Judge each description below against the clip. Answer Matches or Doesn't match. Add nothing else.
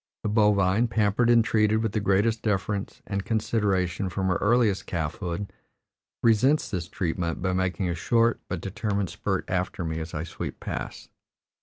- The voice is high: Doesn't match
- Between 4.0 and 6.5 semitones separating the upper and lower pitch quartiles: Doesn't match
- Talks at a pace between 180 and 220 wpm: Doesn't match